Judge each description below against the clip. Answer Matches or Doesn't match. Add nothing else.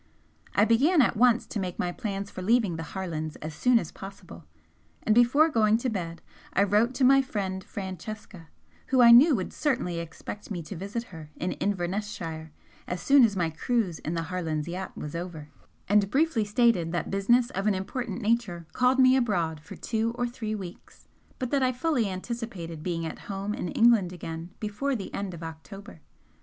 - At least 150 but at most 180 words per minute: Doesn't match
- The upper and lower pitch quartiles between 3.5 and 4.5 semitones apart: Doesn't match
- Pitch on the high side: Matches